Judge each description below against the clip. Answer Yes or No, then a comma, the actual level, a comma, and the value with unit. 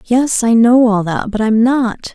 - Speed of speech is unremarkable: No, fast, 250 wpm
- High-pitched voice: Yes, high, 230 Hz